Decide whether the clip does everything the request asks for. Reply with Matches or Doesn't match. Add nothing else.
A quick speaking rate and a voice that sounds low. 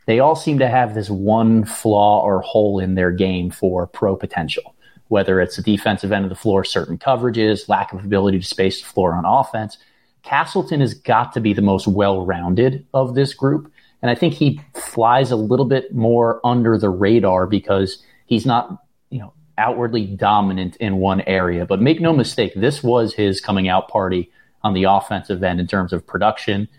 Doesn't match